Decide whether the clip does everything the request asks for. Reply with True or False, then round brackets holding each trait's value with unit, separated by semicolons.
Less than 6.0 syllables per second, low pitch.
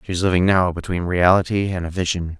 False (6.2 syllables/s; 90 Hz)